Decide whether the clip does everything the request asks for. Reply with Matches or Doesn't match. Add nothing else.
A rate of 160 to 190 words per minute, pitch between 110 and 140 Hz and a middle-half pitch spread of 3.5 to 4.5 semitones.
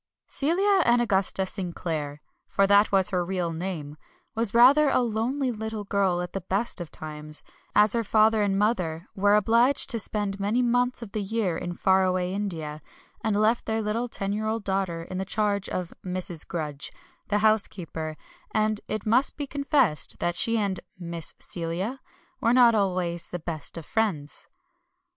Doesn't match